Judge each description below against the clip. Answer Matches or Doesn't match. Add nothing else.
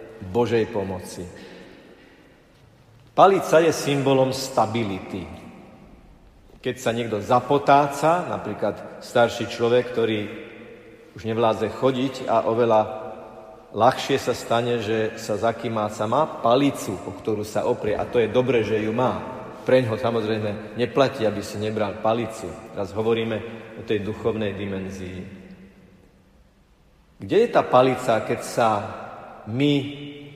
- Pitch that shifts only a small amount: Doesn't match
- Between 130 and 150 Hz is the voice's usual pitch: Doesn't match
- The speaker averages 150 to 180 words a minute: Doesn't match